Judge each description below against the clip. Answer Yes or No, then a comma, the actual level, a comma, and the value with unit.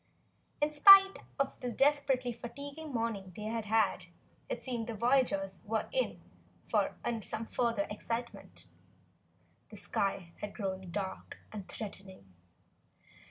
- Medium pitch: No, high, 230 Hz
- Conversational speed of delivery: No, slow, 120 wpm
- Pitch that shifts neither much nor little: Yes, average, 4.7 semitones